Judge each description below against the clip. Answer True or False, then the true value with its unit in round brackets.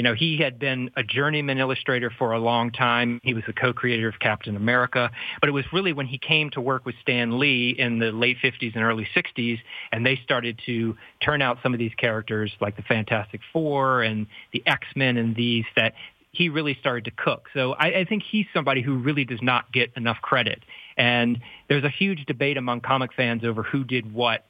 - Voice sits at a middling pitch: False (125 Hz)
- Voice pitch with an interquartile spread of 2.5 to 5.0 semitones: True (2.8 semitones)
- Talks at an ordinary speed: False (215 wpm)